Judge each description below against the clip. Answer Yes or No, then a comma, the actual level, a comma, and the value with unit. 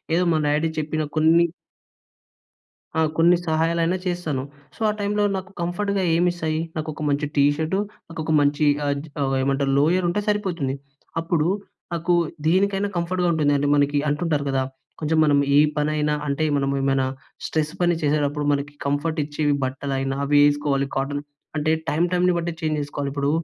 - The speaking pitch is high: No, medium, 155 Hz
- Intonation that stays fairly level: No, average, 3.1 semitones